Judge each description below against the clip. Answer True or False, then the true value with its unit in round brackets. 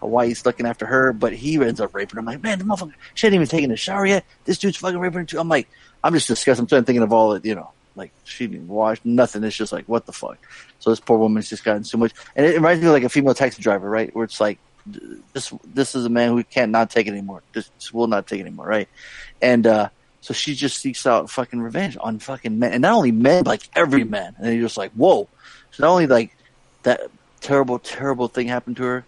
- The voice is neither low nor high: False (120 Hz)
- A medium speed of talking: False (265 wpm)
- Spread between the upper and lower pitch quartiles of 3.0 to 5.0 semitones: True (4.1 semitones)